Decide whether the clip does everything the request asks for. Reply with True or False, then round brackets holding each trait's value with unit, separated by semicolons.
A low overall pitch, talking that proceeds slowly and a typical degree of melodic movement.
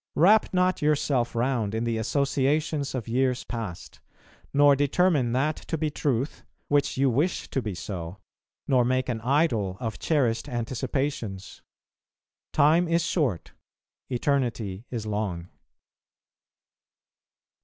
True (130 Hz; 120 wpm; 4.3 semitones)